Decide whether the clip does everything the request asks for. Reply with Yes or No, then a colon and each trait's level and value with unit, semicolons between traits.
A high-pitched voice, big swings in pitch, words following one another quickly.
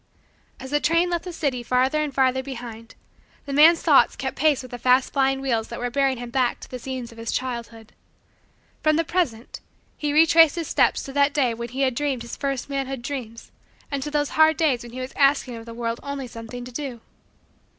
No: very high, 265 Hz; average, 3.4 semitones; fast, 220 wpm